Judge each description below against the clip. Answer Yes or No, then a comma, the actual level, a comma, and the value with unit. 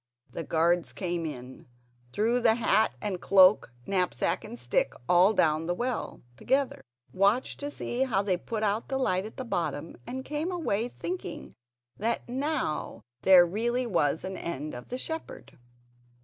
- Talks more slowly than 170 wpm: Yes, average, 160 wpm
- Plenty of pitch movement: Yes, wide, 6.2 semitones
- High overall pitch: Yes, high, 200 Hz